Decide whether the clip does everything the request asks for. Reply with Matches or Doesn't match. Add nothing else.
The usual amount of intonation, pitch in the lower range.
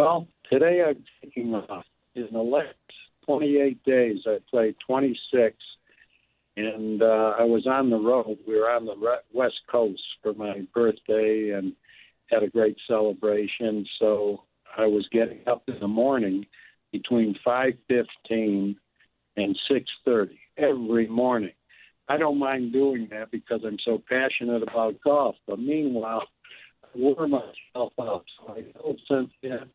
Matches